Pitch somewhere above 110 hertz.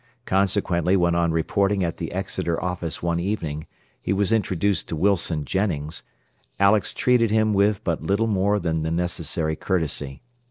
No: very low, 90 Hz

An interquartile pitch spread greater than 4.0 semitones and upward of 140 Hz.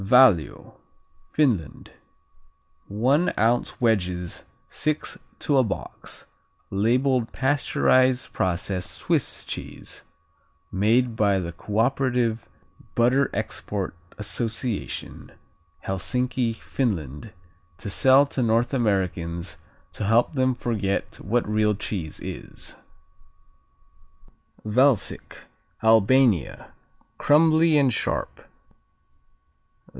No: average, 4.7 semitones; low, 115 Hz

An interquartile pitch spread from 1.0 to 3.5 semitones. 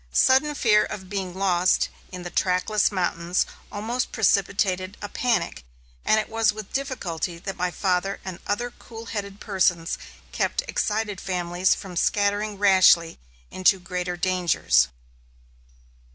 Yes: average, 2.9 semitones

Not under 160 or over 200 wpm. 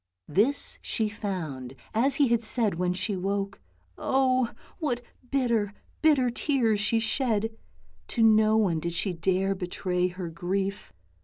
No: average, 140 wpm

